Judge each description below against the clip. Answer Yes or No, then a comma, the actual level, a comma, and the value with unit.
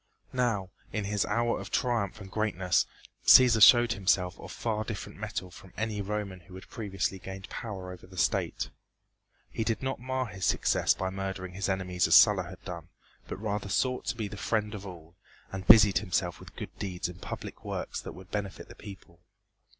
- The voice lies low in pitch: Yes, low, 100 Hz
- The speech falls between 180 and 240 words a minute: Yes, average, 190 wpm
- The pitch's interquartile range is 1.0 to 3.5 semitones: Yes, average, 2.8 semitones